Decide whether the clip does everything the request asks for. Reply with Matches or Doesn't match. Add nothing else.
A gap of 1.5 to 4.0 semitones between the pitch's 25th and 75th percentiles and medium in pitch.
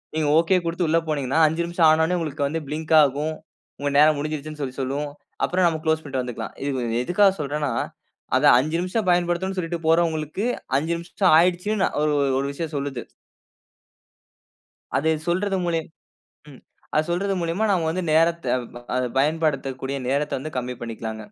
Matches